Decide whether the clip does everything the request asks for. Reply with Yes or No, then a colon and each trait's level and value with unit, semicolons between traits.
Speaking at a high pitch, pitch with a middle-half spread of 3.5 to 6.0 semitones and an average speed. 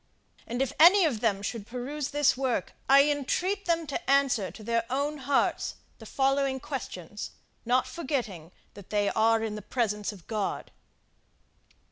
Yes: very high, 255 Hz; average, 5.0 semitones; average, 155 wpm